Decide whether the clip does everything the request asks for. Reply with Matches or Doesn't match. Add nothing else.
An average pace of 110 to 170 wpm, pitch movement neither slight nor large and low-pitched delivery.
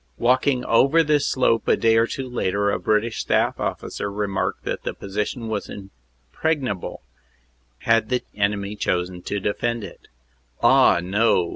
Matches